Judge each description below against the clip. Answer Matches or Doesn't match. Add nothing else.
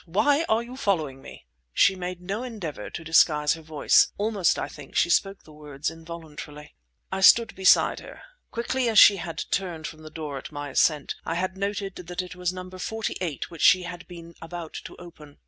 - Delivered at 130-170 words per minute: Doesn't match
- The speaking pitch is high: Doesn't match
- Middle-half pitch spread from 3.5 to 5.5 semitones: Matches